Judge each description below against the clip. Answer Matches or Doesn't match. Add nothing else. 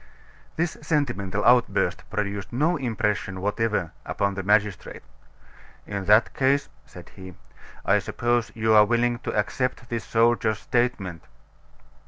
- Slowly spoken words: Matches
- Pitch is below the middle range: Matches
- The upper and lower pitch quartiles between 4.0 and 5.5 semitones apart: Doesn't match